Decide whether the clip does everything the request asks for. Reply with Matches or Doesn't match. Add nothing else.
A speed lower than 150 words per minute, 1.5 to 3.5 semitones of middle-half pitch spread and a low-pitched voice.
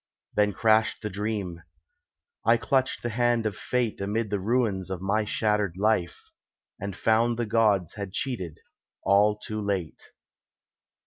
Matches